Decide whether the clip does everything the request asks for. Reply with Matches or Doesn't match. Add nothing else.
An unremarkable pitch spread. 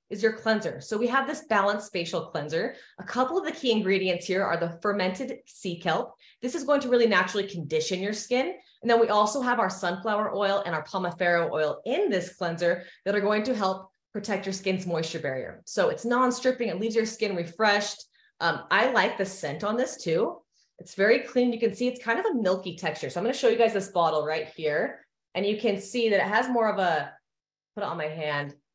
Matches